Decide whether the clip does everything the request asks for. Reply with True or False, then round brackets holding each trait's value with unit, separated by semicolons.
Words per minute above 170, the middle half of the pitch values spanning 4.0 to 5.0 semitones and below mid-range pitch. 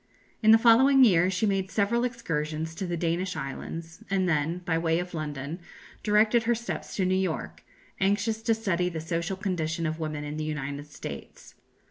False (180 wpm; 4.5 semitones; 180 Hz)